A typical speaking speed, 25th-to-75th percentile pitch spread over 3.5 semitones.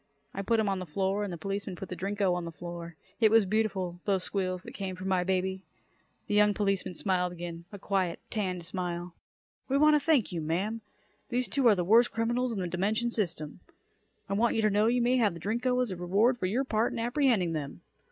No: fast, 230 wpm; average, 4.0 semitones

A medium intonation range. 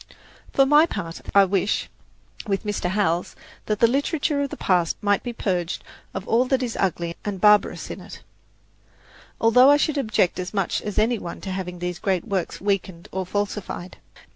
Yes: average, 4.4 semitones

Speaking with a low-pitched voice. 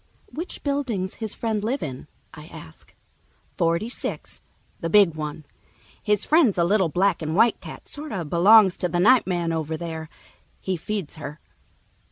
No: medium, 185 Hz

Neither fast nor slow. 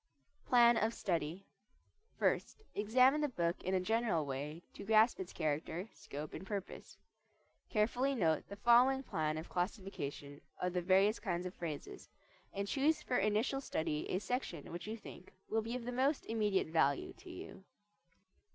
Yes: average, 160 wpm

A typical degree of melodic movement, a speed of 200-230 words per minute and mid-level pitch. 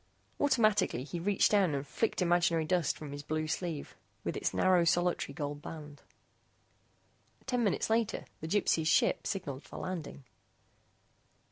No: average, 4.1 semitones; average, 140 wpm; medium, 170 Hz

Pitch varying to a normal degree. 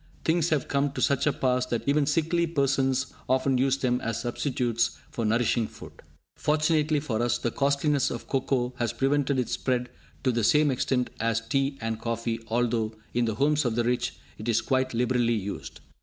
Yes: average, 3.0 semitones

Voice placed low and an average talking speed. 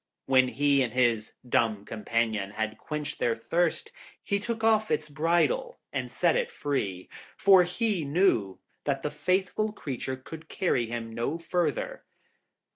No: medium, 145 Hz; average, 145 wpm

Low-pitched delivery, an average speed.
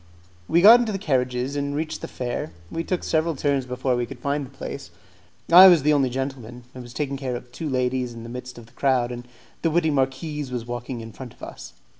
No: low, 130 Hz; fast, 235 wpm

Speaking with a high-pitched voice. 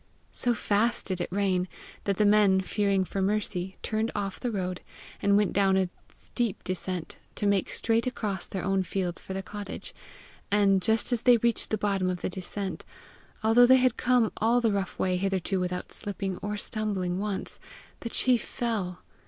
Yes: high, 200 Hz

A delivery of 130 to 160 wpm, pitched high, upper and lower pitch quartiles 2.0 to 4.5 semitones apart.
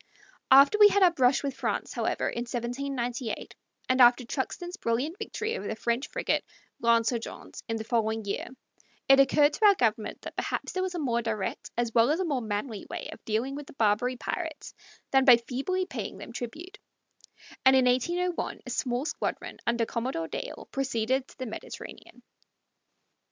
No: average, 175 wpm; very high, 255 Hz; average, 4.0 semitones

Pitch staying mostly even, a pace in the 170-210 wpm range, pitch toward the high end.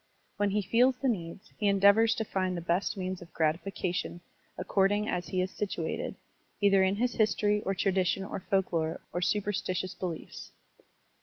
No: narrow, 2.3 semitones; average, 160 wpm; high, 195 Hz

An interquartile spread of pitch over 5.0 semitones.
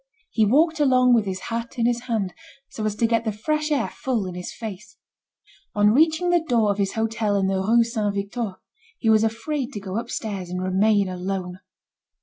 No: average, 3.3 semitones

